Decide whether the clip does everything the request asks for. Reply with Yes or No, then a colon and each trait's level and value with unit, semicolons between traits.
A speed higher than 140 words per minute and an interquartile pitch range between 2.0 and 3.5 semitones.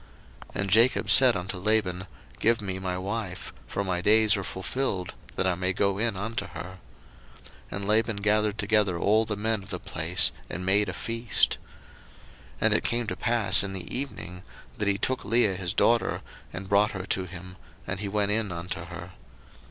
Yes: average, 190 wpm; average, 2.9 semitones